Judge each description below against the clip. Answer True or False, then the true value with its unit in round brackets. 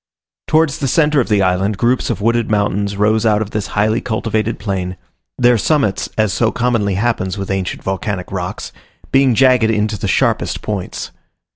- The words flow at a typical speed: True (170 wpm)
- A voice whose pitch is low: True (110 Hz)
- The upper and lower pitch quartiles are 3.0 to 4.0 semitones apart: True (3.3 semitones)